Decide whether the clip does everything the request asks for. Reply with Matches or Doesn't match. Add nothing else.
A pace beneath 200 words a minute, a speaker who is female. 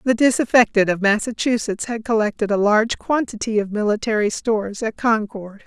Matches